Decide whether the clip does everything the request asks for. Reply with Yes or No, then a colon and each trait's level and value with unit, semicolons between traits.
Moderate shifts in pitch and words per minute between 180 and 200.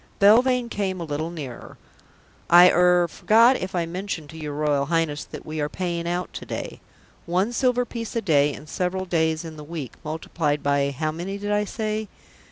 Yes: average, 4.5 semitones; average, 185 wpm